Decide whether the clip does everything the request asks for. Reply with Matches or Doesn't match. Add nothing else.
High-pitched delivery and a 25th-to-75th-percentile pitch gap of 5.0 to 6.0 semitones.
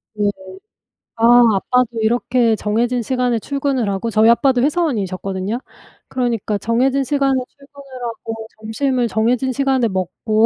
Doesn't match